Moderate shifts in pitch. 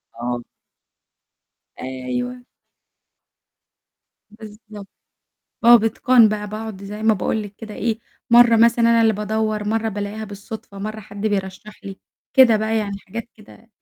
No: narrow, 1.7 semitones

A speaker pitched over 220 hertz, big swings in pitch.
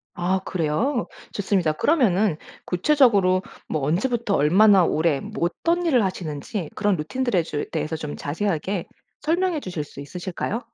No: medium, 185 Hz; wide, 6.3 semitones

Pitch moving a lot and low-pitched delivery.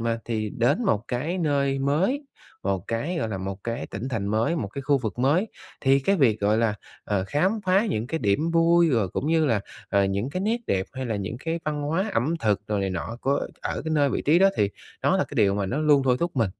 Yes: wide, 7.2 semitones; low, 130 Hz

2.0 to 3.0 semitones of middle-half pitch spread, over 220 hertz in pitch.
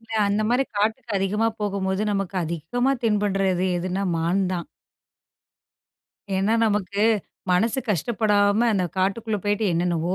No: average, 2.7 semitones; high, 200 Hz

